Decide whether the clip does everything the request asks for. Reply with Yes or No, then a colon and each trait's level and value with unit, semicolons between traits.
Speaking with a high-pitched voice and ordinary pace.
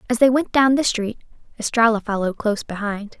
Yes: high, 225 Hz; average, 190 wpm